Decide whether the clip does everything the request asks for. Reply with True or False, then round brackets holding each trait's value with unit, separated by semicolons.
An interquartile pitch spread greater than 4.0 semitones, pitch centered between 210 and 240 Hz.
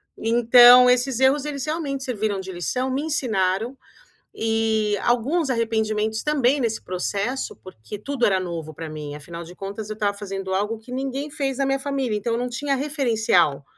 True (5.1 semitones; 230 Hz)